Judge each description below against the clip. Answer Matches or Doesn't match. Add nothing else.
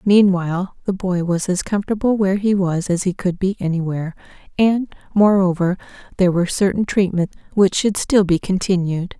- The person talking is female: Matches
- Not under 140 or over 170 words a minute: Matches